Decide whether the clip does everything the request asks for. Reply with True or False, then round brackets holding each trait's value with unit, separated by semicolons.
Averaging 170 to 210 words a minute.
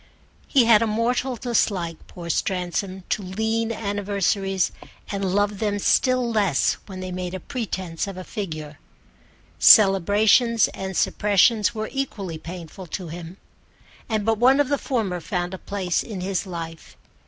False (150 wpm)